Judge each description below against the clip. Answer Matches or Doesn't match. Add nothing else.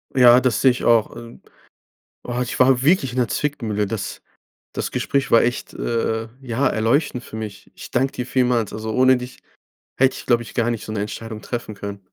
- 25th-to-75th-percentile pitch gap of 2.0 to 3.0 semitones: Matches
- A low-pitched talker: Matches